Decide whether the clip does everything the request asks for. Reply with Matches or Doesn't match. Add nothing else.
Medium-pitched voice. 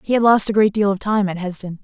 Doesn't match